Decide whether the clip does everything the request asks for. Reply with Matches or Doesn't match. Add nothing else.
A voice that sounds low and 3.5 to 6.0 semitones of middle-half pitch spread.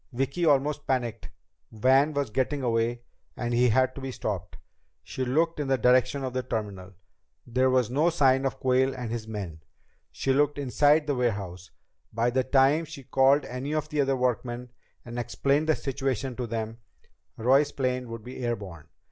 Doesn't match